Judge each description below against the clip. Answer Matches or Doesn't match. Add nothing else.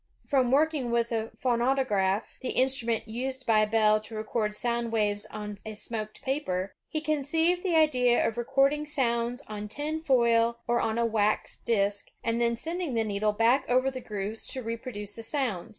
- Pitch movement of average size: Matches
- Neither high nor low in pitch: Doesn't match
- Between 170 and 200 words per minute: Matches